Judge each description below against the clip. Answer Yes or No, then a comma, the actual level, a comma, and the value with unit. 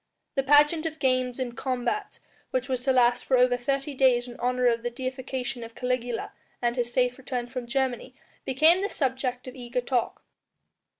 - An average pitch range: No, narrow, 1.5 semitones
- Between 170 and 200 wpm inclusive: Yes, average, 180 wpm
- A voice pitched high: Yes, very high, 255 Hz